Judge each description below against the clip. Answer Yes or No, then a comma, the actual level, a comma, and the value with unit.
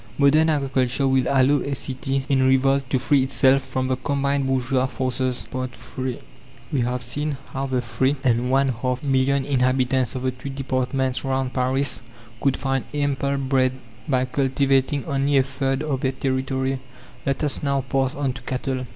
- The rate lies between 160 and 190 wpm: Yes, average, 170 wpm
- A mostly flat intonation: Yes, narrow, 1.2 semitones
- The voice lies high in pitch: No, low, 135 Hz